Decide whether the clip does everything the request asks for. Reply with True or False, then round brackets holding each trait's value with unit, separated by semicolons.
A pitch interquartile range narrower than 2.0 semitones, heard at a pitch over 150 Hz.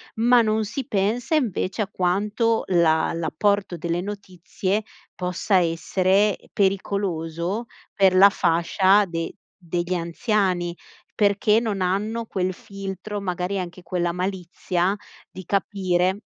False (2.6 semitones; 190 Hz)